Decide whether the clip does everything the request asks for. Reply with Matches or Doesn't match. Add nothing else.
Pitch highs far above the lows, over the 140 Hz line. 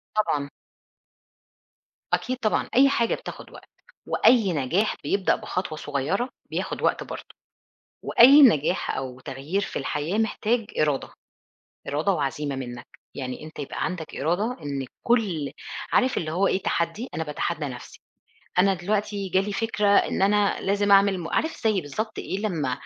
Matches